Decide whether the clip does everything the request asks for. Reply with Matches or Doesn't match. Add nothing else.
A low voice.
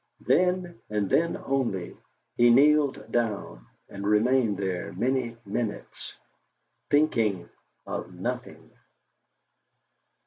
Matches